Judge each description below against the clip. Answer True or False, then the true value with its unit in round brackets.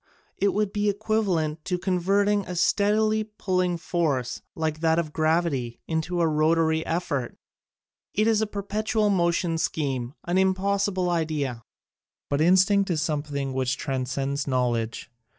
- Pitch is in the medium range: True (170 Hz)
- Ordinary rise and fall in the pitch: True (5.0 semitones)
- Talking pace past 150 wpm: False (135 wpm)